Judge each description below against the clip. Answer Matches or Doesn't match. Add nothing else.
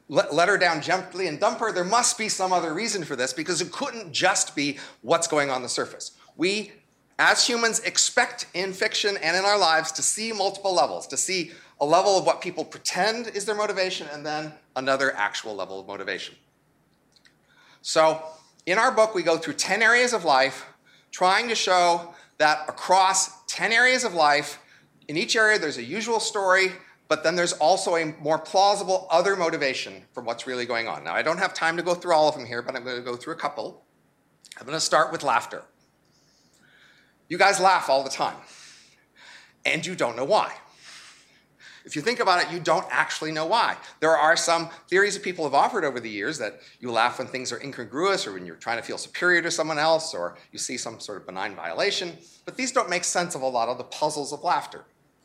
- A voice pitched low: Doesn't match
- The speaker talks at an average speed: Doesn't match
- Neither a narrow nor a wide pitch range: Matches